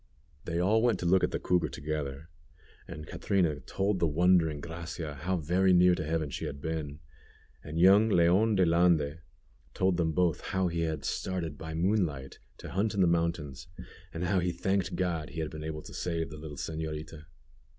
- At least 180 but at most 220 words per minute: Yes, average, 190 wpm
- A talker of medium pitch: No, very low, 85 Hz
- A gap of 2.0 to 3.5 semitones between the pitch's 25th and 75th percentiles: Yes, average, 2.8 semitones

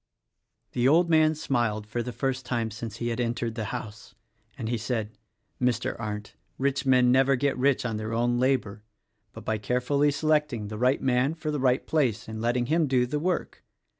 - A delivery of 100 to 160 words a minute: No, average, 195 wpm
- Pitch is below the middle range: Yes, low, 125 Hz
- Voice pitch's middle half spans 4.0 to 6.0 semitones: No, average, 3.3 semitones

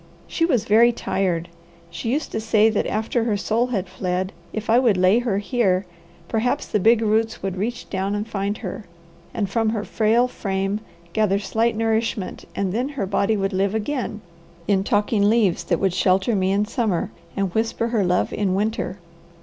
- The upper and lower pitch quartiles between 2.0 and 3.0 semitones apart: Yes, average, 2.7 semitones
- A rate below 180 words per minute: No, average, 185 wpm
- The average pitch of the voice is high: Yes, high, 210 Hz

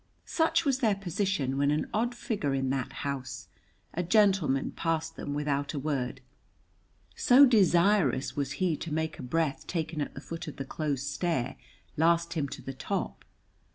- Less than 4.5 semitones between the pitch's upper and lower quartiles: No, average, 5.3 semitones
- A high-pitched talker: No, medium, 155 Hz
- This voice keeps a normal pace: Yes, average, 170 wpm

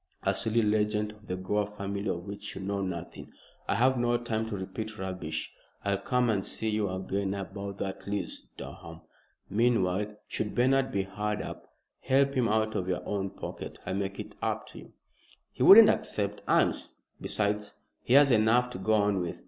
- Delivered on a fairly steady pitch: Yes, narrow, 2.3 semitones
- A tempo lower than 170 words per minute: No, average, 185 wpm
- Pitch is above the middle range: No, low, 105 Hz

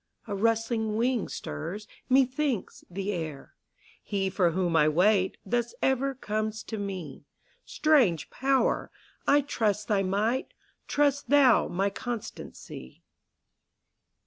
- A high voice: Yes, high, 215 Hz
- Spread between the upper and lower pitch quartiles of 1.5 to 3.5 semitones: No, average, 5.1 semitones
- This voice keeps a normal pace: No, slow, 115 wpm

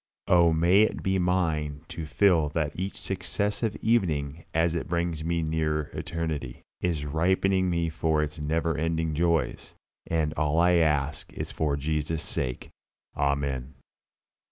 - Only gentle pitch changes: Yes, narrow, 2.3 semitones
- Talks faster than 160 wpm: No, average, 140 wpm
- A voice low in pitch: Yes, very low, 80 Hz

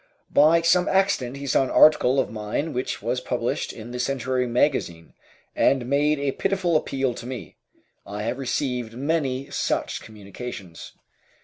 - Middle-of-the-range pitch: No, low, 130 Hz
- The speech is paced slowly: No, average, 150 wpm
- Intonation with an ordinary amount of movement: Yes, average, 3.4 semitones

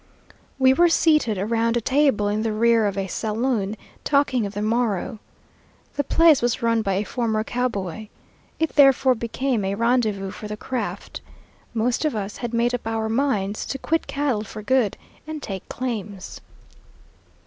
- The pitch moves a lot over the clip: No, average, 3.7 semitones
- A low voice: No, high, 230 Hz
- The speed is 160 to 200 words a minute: Yes, average, 165 wpm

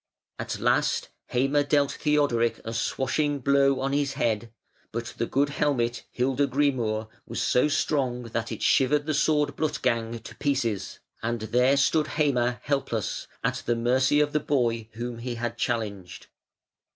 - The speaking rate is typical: Yes, average, 150 wpm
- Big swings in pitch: No, average, 3.5 semitones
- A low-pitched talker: Yes, low, 130 Hz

